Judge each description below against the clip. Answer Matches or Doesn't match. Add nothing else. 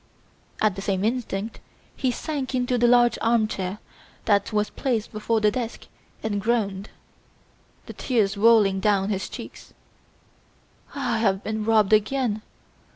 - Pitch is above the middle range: Matches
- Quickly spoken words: Doesn't match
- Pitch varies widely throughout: Doesn't match